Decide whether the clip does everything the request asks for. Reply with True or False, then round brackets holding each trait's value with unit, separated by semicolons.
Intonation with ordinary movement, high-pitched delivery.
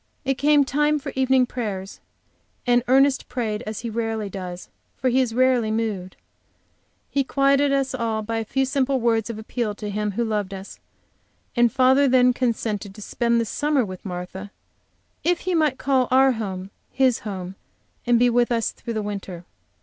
True (3.9 semitones; 235 Hz)